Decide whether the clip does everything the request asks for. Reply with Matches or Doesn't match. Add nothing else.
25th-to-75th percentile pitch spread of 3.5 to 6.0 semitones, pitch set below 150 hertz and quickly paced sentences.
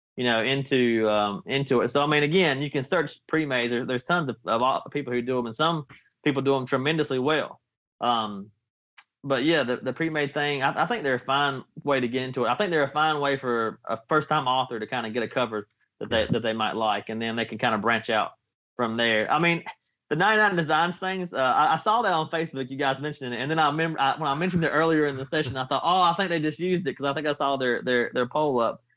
Matches